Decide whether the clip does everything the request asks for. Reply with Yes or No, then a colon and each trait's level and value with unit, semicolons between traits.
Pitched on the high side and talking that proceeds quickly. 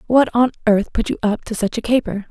Yes: high, 225 Hz; fast, 260 wpm